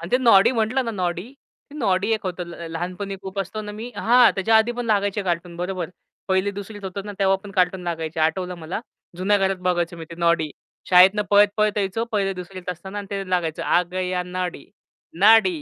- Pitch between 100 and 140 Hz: No, high, 190 Hz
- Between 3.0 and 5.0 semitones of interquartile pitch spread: No, narrow, 2.6 semitones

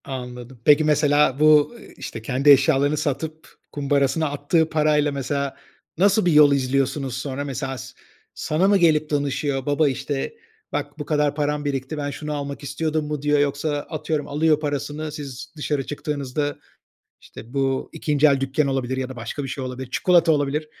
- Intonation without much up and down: Yes, narrow, 2.0 semitones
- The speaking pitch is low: No, medium, 145 Hz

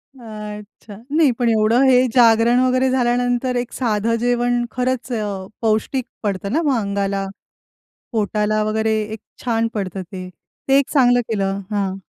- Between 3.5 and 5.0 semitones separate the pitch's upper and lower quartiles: No, average, 2.9 semitones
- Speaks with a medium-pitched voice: No, high, 230 Hz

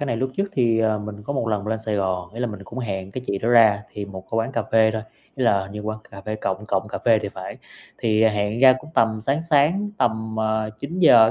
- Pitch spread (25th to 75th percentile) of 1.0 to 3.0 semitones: Yes, narrow, 2.6 semitones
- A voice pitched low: Yes, low, 110 Hz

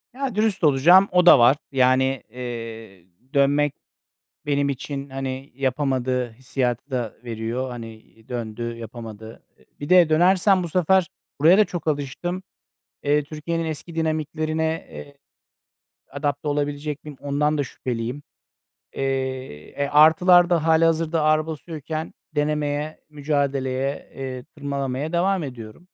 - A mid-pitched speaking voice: Yes, medium, 145 Hz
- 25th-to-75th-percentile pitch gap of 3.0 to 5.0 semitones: Yes, average, 3.5 semitones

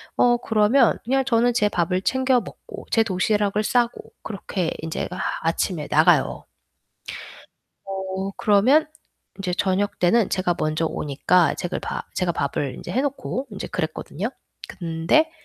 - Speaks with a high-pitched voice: Yes, high, 200 Hz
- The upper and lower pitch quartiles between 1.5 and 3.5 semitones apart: No, wide, 5.4 semitones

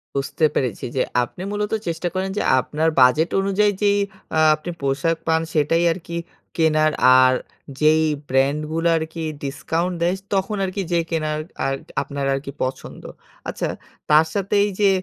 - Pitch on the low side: No, medium, 160 Hz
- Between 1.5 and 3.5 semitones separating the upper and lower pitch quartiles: No, average, 4.1 semitones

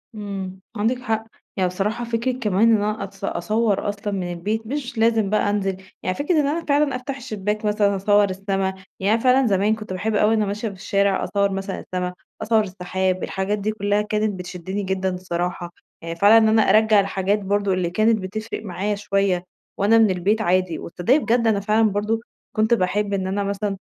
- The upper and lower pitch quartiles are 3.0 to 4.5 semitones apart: No, narrow, 2.5 semitones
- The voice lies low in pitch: No, high, 205 Hz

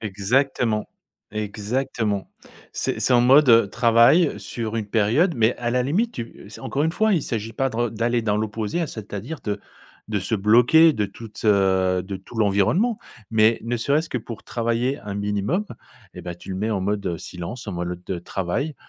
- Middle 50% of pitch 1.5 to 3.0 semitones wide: No, average, 3.7 semitones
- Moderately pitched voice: No, low, 110 Hz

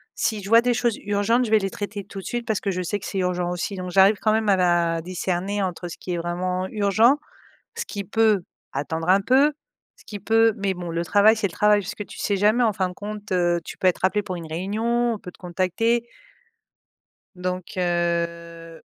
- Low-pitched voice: No, high, 195 Hz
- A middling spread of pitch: Yes, average, 3.3 semitones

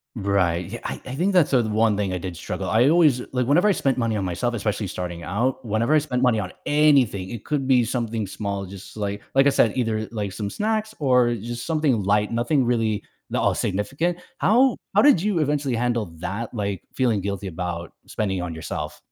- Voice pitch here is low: Yes, low, 115 Hz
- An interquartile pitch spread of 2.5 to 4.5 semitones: No, average, 5.2 semitones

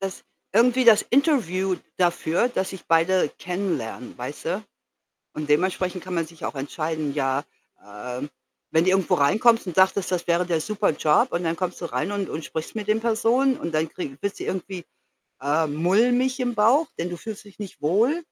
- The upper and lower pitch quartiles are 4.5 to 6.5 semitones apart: Yes, average, 5.1 semitones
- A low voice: No, medium, 185 Hz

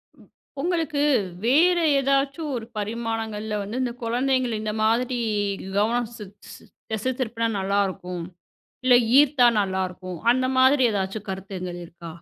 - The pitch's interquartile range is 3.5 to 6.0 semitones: Yes, average, 4.6 semitones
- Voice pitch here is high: Yes, high, 230 Hz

